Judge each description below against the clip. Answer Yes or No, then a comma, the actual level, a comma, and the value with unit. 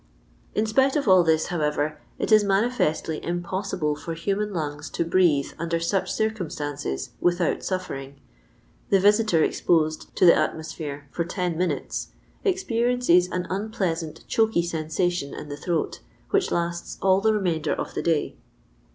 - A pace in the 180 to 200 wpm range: No, average, 150 wpm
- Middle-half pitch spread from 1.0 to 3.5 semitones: No, average, 4.2 semitones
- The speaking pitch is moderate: Yes, medium, 175 Hz